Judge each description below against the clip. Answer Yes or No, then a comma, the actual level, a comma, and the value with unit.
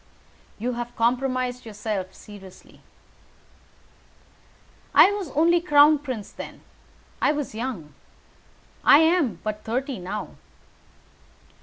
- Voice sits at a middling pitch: No, very high, 250 Hz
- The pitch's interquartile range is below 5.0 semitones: No, wide, 5.5 semitones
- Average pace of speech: No, slow, 100 wpm